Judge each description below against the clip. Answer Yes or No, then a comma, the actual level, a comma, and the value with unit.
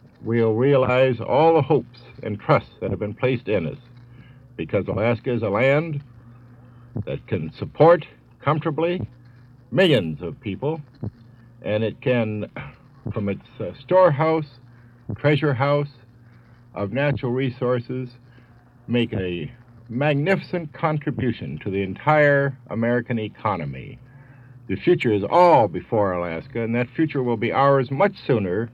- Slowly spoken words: Yes, slow, 125 wpm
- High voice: No, low, 125 Hz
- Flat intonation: No, average, 3.3 semitones